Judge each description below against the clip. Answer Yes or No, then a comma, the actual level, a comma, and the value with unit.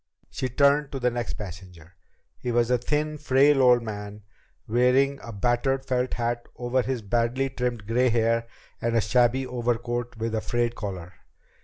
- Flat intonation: Yes, narrow, 2.1 semitones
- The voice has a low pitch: Yes, low, 120 Hz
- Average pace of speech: Yes, average, 165 wpm